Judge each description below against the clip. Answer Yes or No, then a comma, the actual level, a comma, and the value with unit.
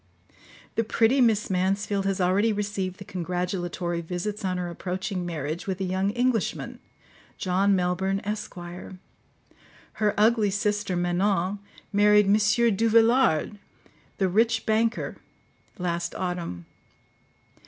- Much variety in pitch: No, average, 2.7 semitones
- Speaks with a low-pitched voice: No, high, 195 Hz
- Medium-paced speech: No, slow, 110 wpm